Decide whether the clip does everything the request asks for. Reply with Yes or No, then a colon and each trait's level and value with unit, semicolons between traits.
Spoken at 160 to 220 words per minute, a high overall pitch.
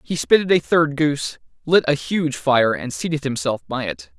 No: average, 200 wpm; medium, 150 Hz